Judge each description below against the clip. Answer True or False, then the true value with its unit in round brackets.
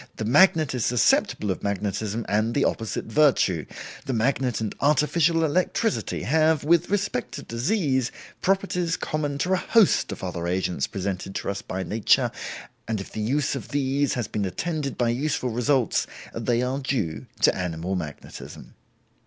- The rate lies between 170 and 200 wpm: False (160 wpm)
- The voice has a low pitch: True (125 Hz)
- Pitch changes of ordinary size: False (6.7 semitones)